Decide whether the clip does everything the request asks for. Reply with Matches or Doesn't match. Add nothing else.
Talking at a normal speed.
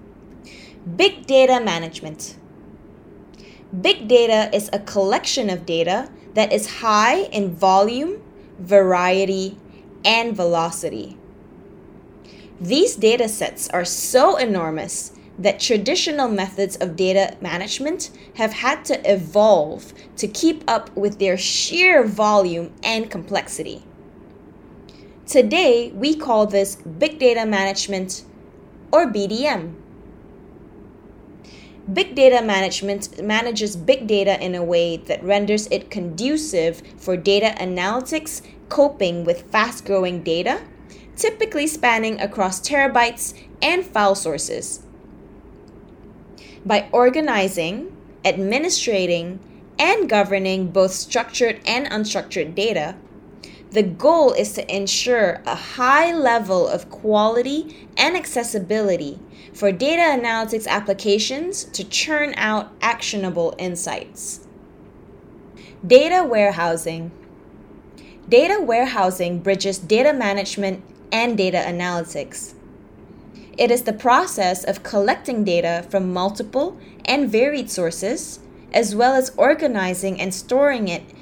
Doesn't match